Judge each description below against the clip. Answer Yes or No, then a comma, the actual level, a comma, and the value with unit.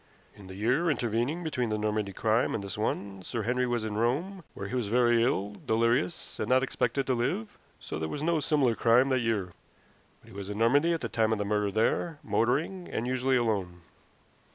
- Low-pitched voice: Yes, low, 115 Hz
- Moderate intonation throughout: Yes, average, 3.7 semitones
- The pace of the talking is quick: Yes, fast, 210 wpm